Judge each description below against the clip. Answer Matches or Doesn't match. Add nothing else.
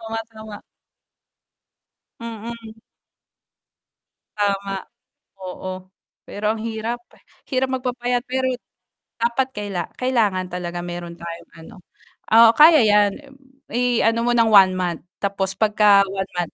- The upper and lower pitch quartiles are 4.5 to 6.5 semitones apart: Doesn't match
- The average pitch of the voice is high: Matches